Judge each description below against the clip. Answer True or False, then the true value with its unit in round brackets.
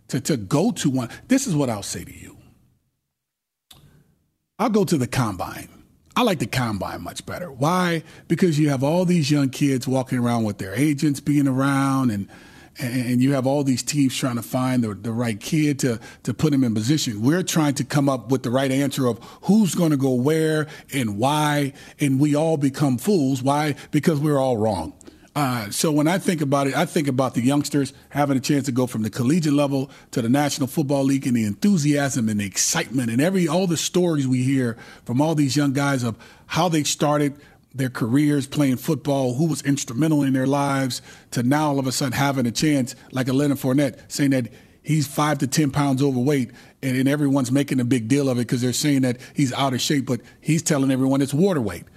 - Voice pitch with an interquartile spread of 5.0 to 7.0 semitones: False (2.7 semitones)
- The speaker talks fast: True (215 wpm)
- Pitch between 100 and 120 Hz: False (140 Hz)